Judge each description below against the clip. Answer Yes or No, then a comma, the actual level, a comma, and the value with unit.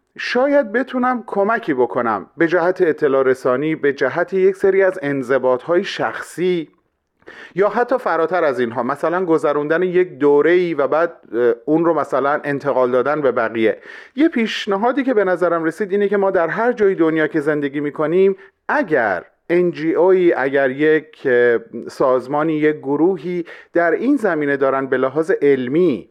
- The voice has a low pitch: No, medium, 165 Hz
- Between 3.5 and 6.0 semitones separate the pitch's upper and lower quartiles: Yes, wide, 5.4 semitones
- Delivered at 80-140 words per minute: No, average, 150 wpm